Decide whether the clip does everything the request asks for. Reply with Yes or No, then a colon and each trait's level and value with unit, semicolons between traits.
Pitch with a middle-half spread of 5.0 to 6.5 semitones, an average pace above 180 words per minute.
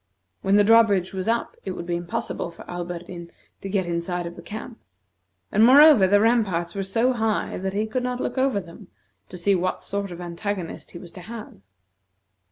No: average, 4.0 semitones; average, 195 wpm